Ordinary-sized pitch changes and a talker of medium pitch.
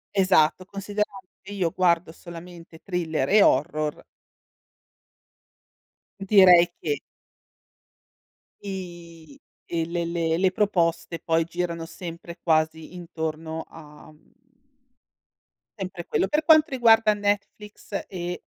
Yes: average, 3.0 semitones; medium, 175 Hz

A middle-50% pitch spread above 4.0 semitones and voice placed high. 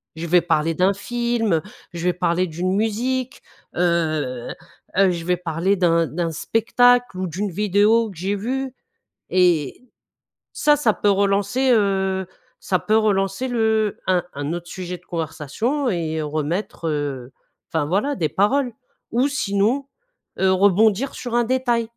Yes: average, 5.0 semitones; high, 195 Hz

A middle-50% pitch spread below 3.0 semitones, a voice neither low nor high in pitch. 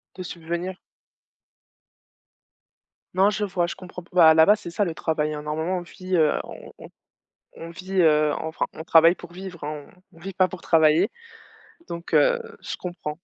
Yes: narrow, 2.6 semitones; medium, 170 Hz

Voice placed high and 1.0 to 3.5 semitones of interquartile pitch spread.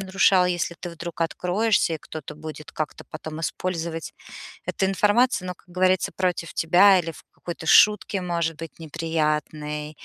No: medium, 170 Hz; average, 2.7 semitones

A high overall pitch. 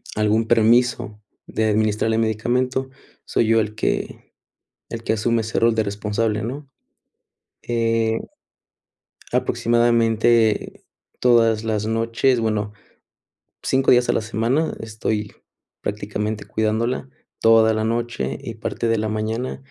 No: low, 115 Hz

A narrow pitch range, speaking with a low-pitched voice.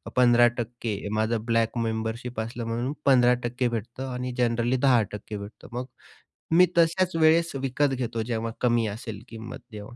Yes: narrow, 2.1 semitones; low, 120 Hz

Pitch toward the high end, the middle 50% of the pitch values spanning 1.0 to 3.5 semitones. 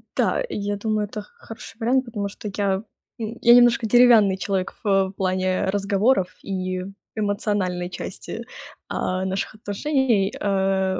Yes: high, 200 Hz; average, 2.8 semitones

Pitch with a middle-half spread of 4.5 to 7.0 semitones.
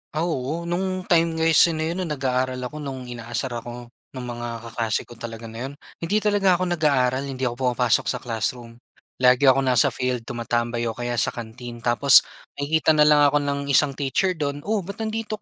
Yes: average, 4.8 semitones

